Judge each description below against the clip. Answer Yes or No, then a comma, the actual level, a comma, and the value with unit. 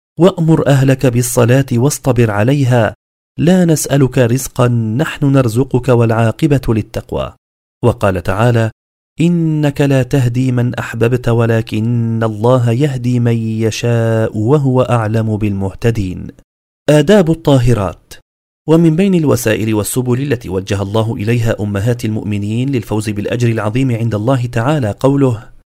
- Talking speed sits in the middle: Yes, average, 105 wpm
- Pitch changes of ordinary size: Yes, average, 3.5 semitones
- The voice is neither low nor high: No, low, 120 Hz